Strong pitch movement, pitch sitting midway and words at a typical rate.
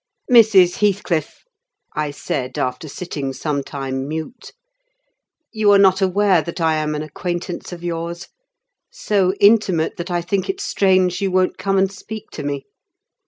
No: average, 4.2 semitones; medium, 175 Hz; average, 155 wpm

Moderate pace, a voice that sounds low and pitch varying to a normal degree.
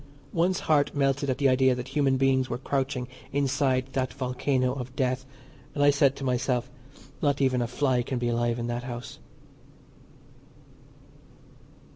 No: average, 155 wpm; low, 130 Hz; narrow, 1.8 semitones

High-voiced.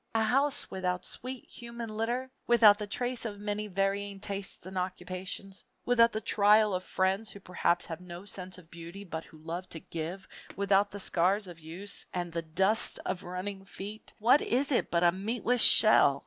Yes: high, 195 Hz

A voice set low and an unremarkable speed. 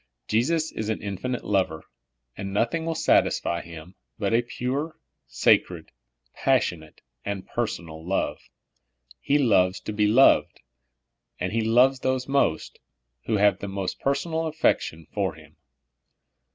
No: low, 110 Hz; slow, 130 wpm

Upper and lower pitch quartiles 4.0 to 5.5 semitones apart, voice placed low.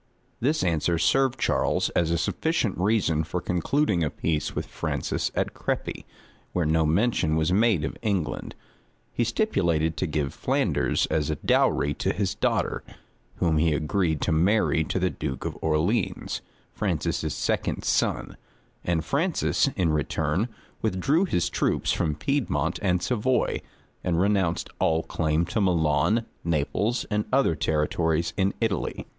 Yes: average, 5.2 semitones; very low, 85 Hz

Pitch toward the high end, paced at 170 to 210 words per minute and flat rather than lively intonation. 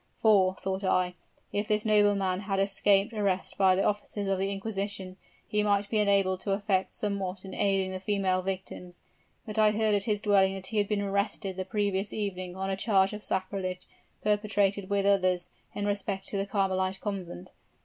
Yes: high, 195 Hz; average, 185 wpm; narrow, 1.4 semitones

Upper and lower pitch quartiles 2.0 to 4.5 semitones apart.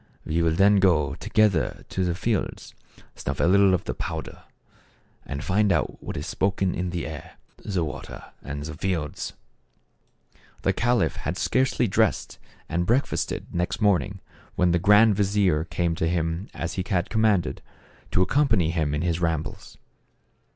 Yes: average, 3.6 semitones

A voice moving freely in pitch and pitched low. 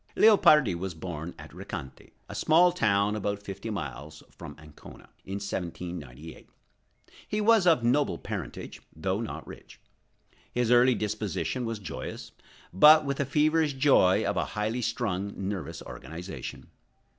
Yes: wide, 7.1 semitones; low, 105 Hz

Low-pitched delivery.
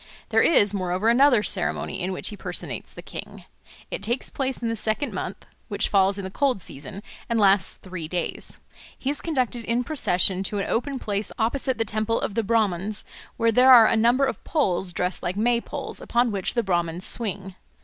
No: high, 215 Hz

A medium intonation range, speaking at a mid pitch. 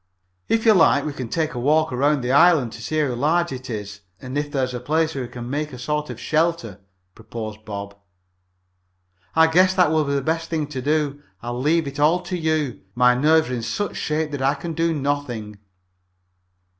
Yes: average, 4.3 semitones; medium, 145 Hz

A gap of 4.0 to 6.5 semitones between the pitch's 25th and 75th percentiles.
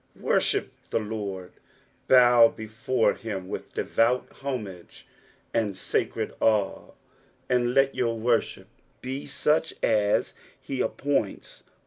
No: average, 3.4 semitones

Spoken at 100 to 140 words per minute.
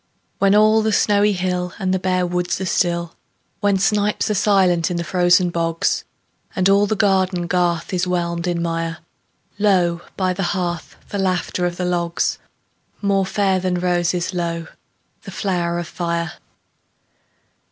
No: average, 155 wpm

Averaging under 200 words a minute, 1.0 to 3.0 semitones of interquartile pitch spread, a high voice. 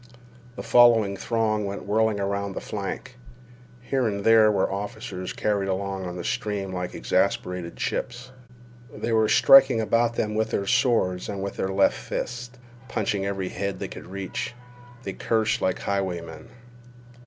No: average, 155 wpm; narrow, 2.6 semitones; low, 100 Hz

